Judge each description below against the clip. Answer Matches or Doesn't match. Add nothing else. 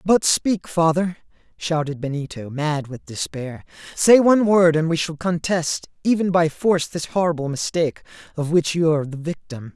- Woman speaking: Doesn't match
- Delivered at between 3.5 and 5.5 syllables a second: Matches